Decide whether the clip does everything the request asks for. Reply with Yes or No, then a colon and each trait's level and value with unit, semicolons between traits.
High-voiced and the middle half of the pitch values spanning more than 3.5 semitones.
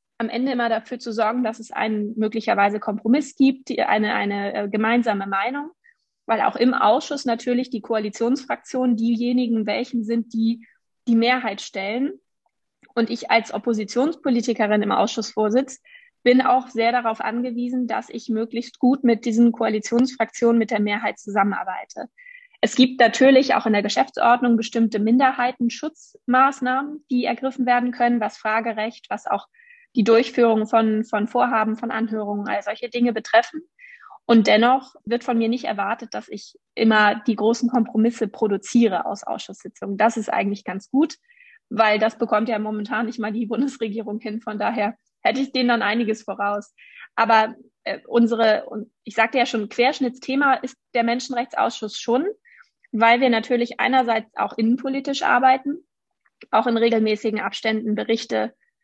No: high, 235 Hz; average, 2.7 semitones